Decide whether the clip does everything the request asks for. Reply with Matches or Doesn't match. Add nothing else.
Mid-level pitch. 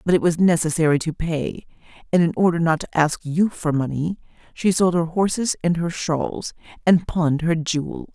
Matches